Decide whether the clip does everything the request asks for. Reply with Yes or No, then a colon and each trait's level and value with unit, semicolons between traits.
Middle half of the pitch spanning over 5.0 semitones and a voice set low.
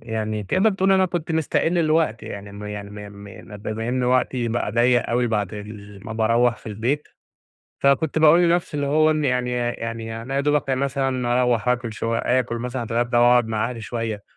No: average, 3.8 semitones; low, 120 Hz